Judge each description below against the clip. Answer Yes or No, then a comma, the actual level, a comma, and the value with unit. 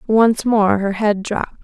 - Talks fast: No, average, 185 wpm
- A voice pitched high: Yes, high, 210 Hz